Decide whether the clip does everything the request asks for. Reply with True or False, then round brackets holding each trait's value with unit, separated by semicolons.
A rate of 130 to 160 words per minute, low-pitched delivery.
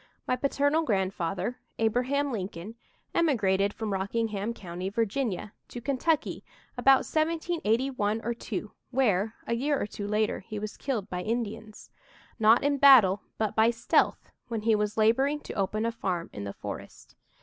False (150 wpm; 225 Hz)